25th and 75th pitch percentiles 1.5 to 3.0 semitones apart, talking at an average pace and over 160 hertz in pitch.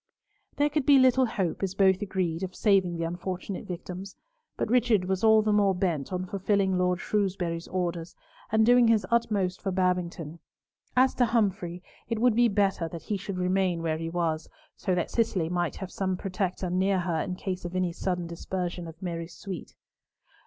Yes: average, 2.7 semitones; average, 185 wpm; medium, 185 Hz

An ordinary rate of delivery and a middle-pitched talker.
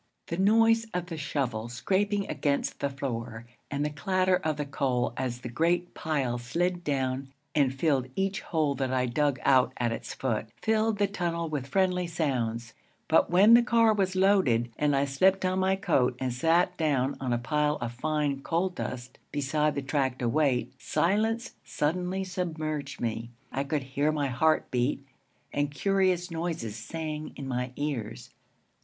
Yes: average, 170 wpm; medium, 150 Hz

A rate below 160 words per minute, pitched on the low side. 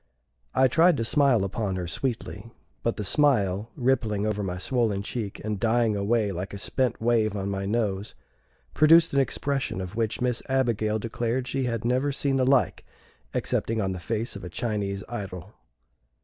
No: average, 175 wpm; low, 115 Hz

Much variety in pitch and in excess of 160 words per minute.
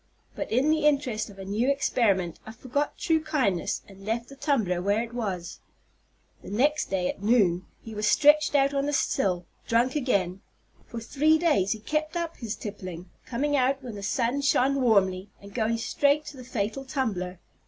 Yes: wide, 5.9 semitones; average, 185 wpm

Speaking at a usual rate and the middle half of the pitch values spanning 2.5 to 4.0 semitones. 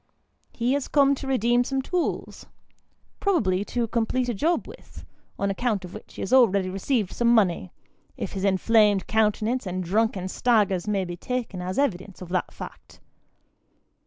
No: average, 160 wpm; average, 4.7 semitones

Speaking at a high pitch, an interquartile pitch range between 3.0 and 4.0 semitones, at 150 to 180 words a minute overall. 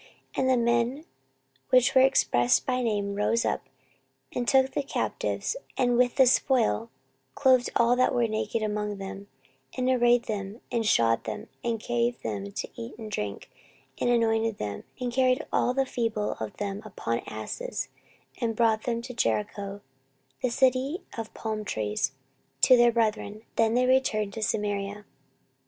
Yes: high, 230 Hz; average, 3.4 semitones; average, 165 wpm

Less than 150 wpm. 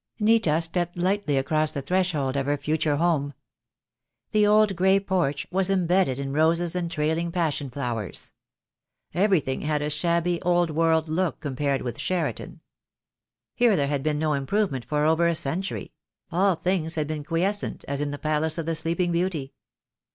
No: average, 165 wpm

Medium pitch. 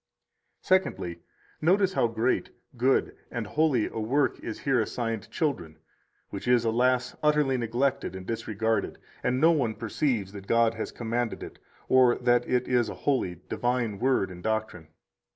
No: low, 120 Hz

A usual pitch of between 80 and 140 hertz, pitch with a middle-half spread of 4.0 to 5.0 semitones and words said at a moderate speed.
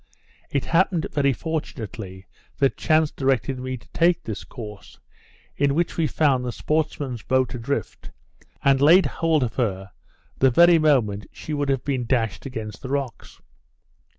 Yes: low, 135 Hz; average, 4.5 semitones; average, 150 wpm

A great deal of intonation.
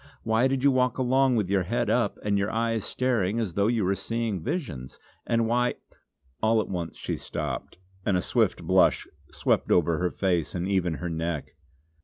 No: average, 4.9 semitones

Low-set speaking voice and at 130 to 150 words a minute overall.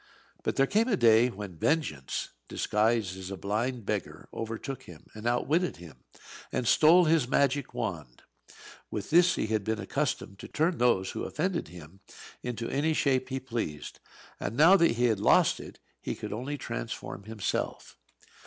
No: low, 120 Hz; average, 165 wpm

